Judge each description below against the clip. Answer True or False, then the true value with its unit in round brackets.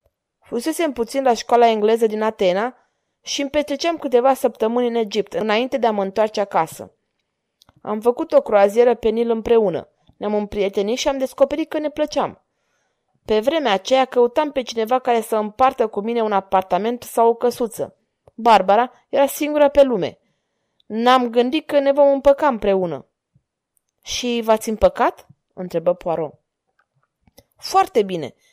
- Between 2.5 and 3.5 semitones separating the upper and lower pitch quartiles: False (4.2 semitones)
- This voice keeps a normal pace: True (150 wpm)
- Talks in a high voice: True (235 Hz)